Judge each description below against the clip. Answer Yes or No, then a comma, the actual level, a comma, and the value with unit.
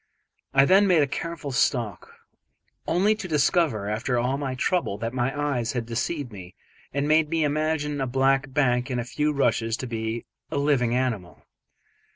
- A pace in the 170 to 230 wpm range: Yes, average, 175 wpm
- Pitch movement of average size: Yes, average, 4.0 semitones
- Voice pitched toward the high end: No, low, 135 Hz